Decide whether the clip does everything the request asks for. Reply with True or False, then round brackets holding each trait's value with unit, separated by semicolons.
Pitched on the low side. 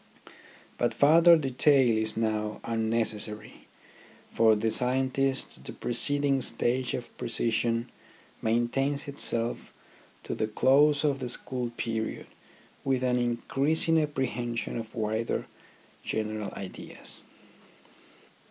True (120 Hz)